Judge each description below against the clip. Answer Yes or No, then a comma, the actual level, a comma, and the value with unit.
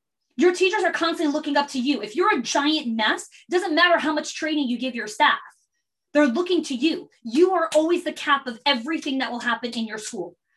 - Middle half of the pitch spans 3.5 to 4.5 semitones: Yes, average, 4.2 semitones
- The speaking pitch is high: Yes, very high, 300 Hz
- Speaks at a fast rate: Yes, fast, 225 wpm